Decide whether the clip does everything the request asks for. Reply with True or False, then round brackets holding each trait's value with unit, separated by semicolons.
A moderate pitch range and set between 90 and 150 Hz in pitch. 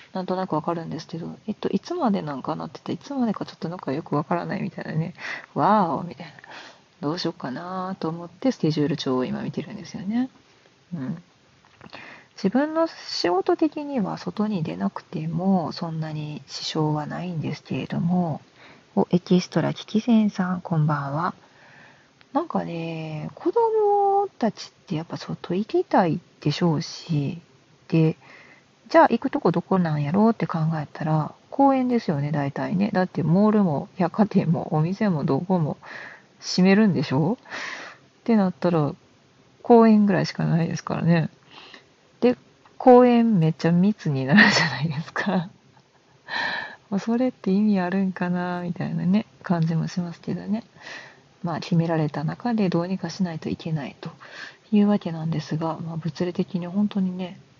False (4.4 semitones; 180 Hz)